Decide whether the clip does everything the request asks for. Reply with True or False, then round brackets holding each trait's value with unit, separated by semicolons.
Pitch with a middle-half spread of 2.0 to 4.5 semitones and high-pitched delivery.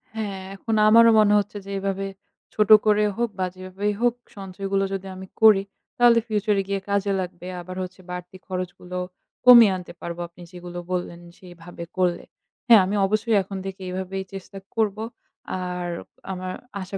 True (2.4 semitones; 195 Hz)